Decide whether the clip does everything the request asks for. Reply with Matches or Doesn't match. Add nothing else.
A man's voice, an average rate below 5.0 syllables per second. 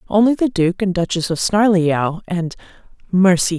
Doesn't match